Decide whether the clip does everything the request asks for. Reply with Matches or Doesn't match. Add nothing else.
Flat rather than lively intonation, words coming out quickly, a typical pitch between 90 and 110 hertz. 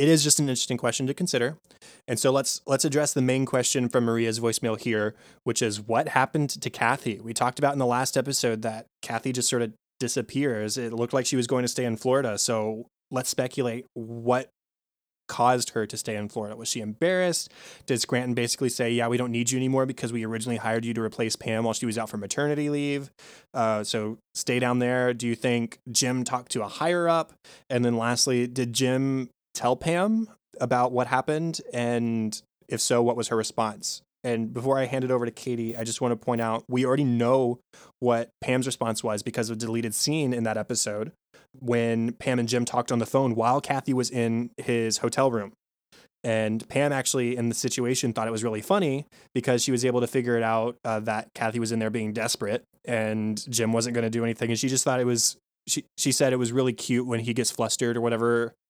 Doesn't match